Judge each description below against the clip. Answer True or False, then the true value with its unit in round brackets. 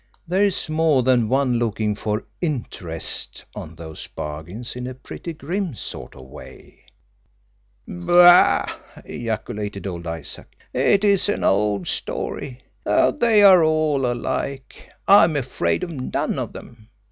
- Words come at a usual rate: False (130 wpm)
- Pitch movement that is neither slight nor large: False (7.9 semitones)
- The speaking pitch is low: True (125 Hz)